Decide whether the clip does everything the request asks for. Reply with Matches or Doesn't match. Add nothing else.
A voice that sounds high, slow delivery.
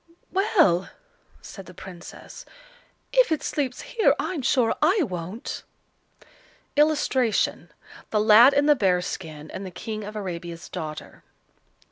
Matches